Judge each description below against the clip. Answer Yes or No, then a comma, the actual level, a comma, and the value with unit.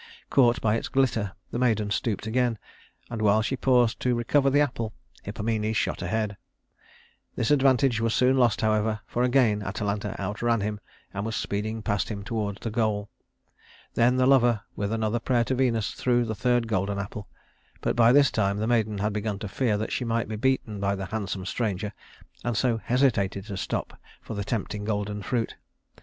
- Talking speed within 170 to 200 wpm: Yes, average, 185 wpm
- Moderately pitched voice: No, low, 110 Hz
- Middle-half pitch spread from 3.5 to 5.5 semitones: No, average, 2.8 semitones